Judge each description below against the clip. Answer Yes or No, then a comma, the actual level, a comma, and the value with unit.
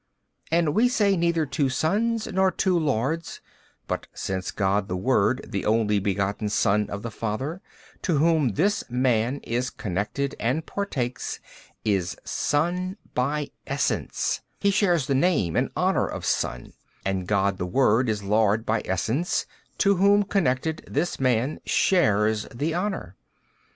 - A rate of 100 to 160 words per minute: Yes, average, 145 wpm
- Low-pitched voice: Yes, low, 130 Hz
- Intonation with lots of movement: Yes, wide, 8.3 semitones